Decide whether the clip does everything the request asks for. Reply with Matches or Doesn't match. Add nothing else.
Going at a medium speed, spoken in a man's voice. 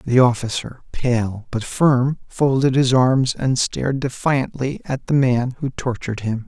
Matches